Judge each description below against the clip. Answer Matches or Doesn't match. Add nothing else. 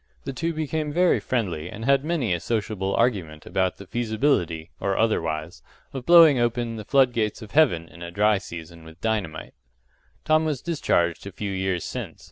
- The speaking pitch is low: Matches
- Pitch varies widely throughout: Matches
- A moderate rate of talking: Matches